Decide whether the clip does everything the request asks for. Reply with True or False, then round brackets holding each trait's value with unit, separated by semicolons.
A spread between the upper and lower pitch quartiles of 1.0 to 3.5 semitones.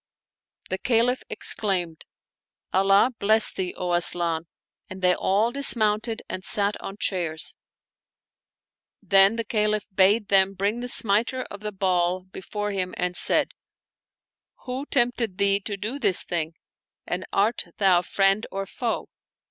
True (2.9 semitones)